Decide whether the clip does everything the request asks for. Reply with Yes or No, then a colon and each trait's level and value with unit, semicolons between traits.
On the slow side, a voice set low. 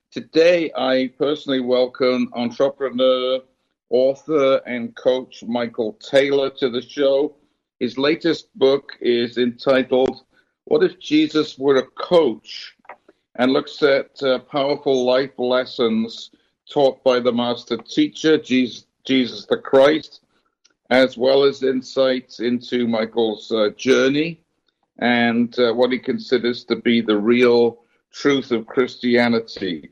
Yes: slow, 120 wpm; low, 130 Hz